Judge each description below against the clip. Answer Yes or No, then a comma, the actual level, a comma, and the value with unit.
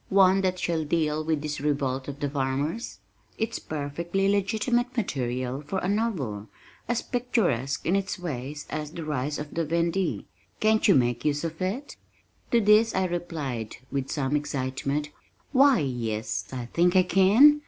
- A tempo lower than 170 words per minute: Yes, average, 160 wpm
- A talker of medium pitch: Yes, medium, 160 Hz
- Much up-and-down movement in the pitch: Yes, wide, 5.9 semitones